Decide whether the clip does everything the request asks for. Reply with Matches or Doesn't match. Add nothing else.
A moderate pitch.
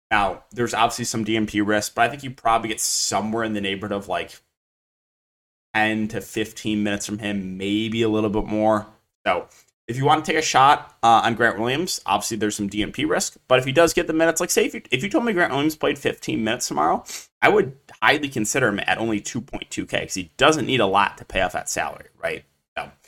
Doesn't match